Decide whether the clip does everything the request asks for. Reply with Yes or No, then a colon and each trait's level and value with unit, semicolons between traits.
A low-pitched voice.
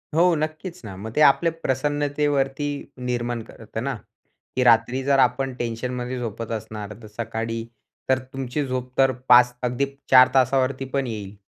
Yes: low, 125 Hz